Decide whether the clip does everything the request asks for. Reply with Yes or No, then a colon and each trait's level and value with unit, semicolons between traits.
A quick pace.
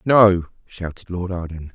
No: average, 140 wpm